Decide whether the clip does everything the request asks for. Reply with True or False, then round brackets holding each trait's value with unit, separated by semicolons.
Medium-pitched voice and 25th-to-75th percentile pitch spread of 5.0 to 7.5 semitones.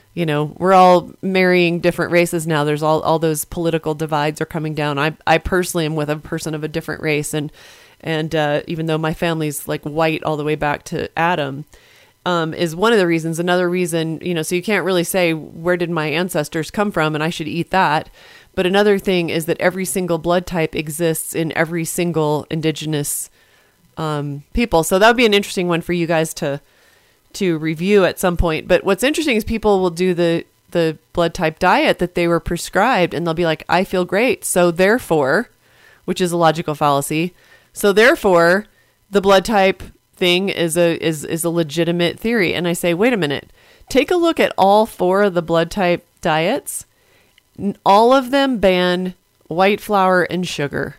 False (170 Hz; 2.6 semitones)